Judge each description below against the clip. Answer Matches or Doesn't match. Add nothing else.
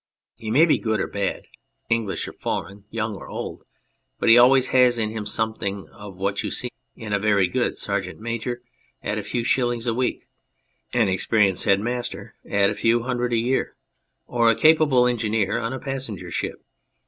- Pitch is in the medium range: Doesn't match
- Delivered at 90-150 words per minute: Doesn't match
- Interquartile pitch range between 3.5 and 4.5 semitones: Doesn't match